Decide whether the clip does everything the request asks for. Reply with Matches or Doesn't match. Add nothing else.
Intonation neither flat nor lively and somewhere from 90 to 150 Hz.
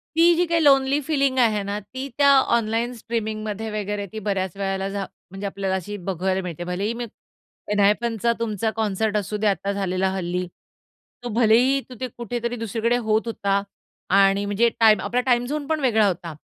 Doesn't match